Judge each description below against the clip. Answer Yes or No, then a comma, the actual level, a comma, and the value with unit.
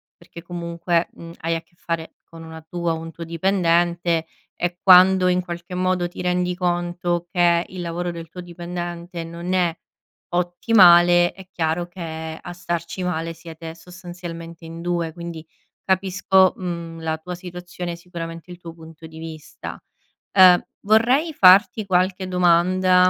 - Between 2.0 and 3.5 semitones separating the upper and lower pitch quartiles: No, narrow, 1.4 semitones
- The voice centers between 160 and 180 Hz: Yes, medium, 175 Hz